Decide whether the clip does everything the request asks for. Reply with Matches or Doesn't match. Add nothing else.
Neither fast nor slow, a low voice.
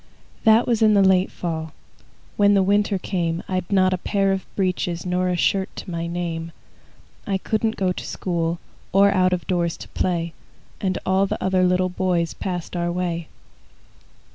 Doesn't match